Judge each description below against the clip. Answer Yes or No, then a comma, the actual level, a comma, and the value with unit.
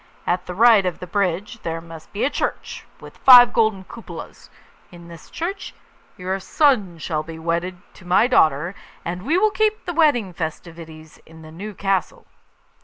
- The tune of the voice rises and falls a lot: Yes, wide, 5.7 semitones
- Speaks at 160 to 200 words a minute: Yes, average, 175 wpm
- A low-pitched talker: No, medium, 185 Hz